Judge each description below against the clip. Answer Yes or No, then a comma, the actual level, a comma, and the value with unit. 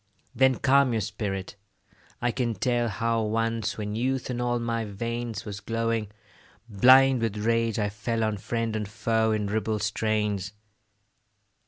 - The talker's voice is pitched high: No, low, 115 Hz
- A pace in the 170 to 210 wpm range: No, average, 150 wpm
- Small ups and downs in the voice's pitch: Yes, narrow, 1.9 semitones